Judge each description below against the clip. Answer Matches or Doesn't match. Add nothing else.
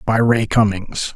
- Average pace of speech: Matches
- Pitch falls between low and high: Doesn't match